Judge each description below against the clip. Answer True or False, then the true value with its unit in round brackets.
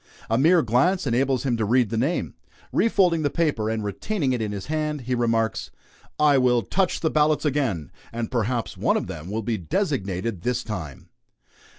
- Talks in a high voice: False (125 Hz)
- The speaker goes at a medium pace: True (185 wpm)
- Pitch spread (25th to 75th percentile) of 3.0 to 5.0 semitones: False (5.4 semitones)